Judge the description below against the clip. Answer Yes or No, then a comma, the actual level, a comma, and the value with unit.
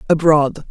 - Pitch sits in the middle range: Yes, medium, 150 Hz